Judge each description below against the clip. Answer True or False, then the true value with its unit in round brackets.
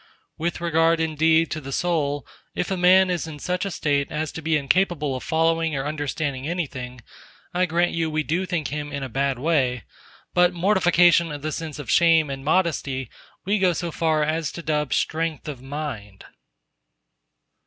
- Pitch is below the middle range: False (155 Hz)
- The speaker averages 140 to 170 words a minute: False (180 wpm)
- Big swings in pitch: False (3.1 semitones)